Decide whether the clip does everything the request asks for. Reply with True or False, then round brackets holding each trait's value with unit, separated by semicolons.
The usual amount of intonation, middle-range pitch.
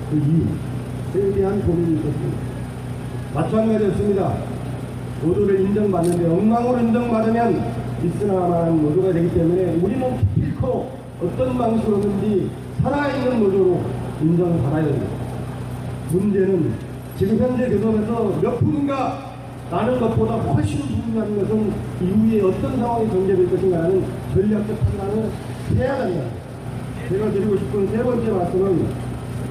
False (7.8 semitones; 175 Hz)